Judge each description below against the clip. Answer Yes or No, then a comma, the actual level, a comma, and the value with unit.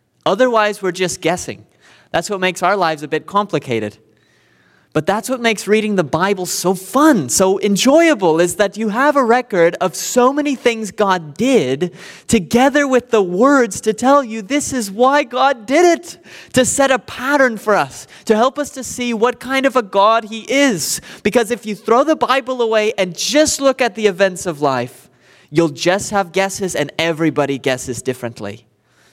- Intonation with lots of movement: Yes, wide, 6.4 semitones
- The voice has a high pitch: Yes, high, 210 Hz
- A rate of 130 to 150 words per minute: No, average, 185 wpm